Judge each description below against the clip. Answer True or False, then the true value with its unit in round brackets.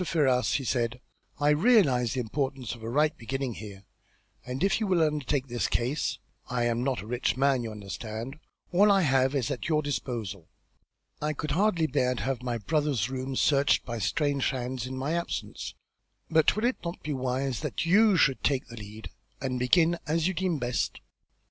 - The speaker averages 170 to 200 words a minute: True (190 wpm)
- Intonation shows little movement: False (3.9 semitones)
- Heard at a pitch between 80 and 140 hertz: True (135 Hz)